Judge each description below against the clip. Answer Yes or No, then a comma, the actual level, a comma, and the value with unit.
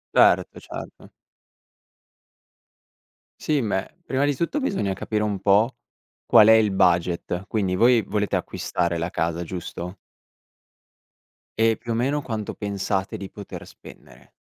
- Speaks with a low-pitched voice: Yes, low, 105 Hz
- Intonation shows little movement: No, average, 3.6 semitones